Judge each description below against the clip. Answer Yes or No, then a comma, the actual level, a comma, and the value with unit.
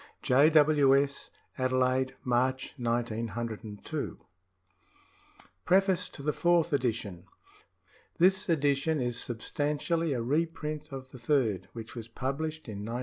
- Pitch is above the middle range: No, low, 135 Hz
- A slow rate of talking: Yes, slow, 115 wpm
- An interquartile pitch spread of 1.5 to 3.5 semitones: No, average, 4.5 semitones